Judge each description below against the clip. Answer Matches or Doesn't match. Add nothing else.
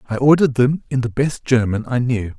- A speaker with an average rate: Doesn't match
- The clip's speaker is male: Matches